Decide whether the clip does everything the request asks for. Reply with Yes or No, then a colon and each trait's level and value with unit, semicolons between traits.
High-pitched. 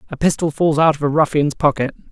No: medium, 150 Hz